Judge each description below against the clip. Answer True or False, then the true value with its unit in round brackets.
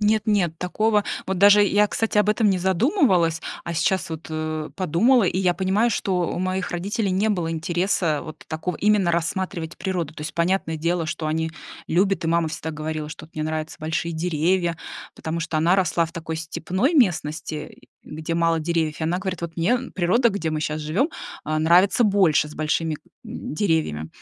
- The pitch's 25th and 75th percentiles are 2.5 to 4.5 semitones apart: True (3.3 semitones)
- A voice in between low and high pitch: True (170 Hz)